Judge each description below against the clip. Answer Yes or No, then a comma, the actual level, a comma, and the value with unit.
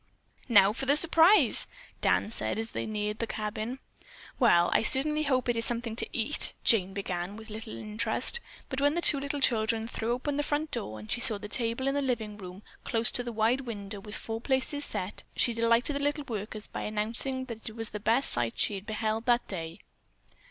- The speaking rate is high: Yes, fast, 210 wpm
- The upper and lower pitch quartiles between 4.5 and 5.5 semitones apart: No, average, 3.7 semitones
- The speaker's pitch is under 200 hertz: No, high, 230 Hz